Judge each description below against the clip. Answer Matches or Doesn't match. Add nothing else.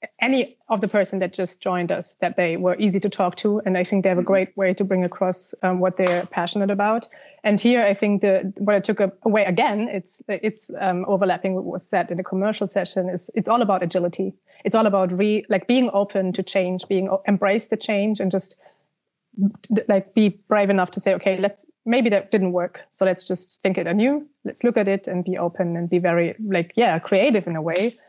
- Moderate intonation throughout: Doesn't match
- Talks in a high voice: Matches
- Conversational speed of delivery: Doesn't match